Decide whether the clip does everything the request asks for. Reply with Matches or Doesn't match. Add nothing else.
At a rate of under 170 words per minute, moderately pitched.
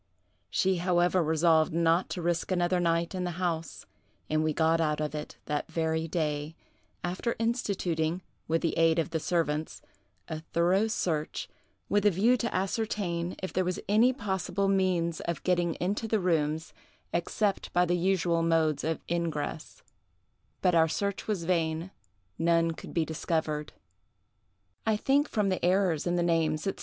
Matches